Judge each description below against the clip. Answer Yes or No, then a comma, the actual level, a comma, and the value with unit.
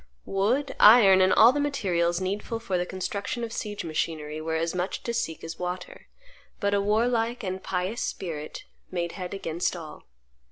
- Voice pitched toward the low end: No, high, 190 Hz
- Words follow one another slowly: No, average, 170 wpm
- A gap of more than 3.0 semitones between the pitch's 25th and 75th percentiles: Yes, average, 4.5 semitones